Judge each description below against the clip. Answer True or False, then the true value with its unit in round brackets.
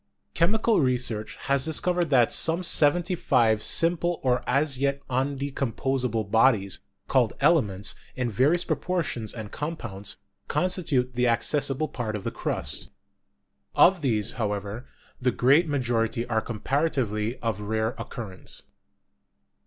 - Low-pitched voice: True (130 Hz)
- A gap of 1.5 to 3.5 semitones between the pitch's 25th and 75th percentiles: False (5.1 semitones)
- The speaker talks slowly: True (120 wpm)